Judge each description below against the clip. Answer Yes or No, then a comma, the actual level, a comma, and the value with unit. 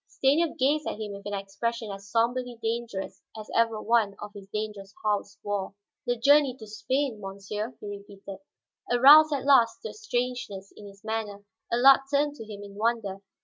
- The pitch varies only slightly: No, average, 3.6 semitones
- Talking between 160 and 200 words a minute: Yes, average, 180 wpm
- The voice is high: Yes, high, 220 Hz